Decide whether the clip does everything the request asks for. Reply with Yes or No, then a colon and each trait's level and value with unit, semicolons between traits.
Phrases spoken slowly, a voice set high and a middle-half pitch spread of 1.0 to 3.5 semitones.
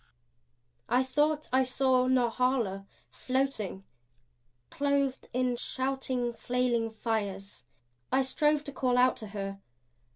Yes: slow, 105 wpm; very high, 255 Hz; average, 2.9 semitones